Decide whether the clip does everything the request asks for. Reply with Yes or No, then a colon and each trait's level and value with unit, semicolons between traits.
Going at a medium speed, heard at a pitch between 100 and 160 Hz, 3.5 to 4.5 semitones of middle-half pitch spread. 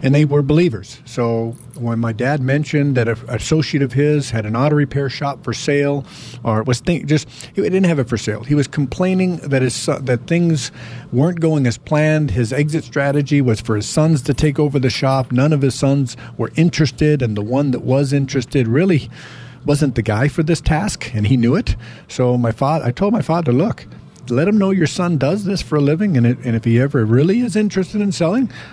No: fast, 225 wpm; medium, 140 Hz; average, 4.1 semitones